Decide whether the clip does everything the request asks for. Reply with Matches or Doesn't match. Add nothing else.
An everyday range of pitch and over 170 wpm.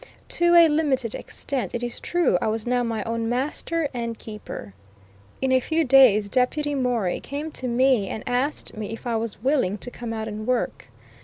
Matches